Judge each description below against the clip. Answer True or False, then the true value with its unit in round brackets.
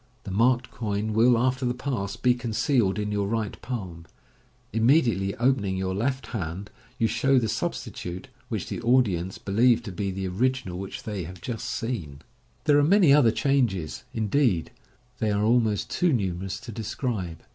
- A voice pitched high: False (110 Hz)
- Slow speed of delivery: False (175 wpm)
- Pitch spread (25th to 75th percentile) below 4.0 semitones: False (4.5 semitones)